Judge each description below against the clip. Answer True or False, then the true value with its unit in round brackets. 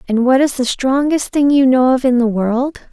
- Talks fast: True (245 wpm)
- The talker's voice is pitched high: True (260 Hz)